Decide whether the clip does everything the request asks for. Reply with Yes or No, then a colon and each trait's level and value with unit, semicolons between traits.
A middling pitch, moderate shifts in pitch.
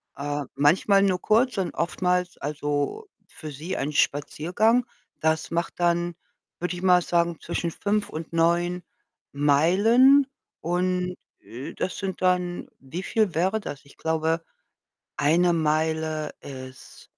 Yes: medium, 170 Hz; average, 3.0 semitones